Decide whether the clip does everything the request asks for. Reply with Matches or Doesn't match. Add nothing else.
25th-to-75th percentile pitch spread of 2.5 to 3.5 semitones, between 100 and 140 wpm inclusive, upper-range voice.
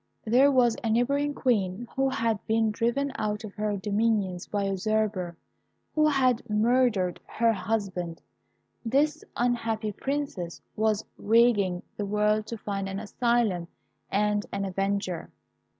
Matches